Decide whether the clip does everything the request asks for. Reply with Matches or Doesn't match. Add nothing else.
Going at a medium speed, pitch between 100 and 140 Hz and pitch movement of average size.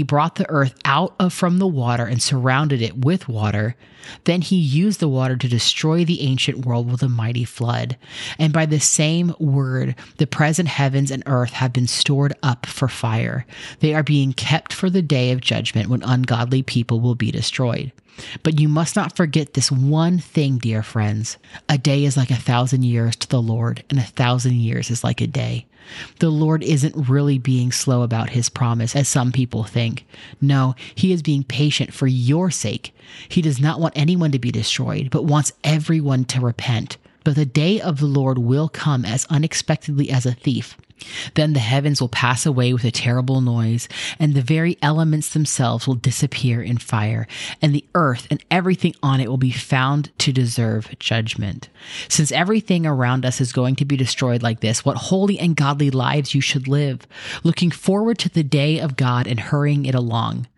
Matches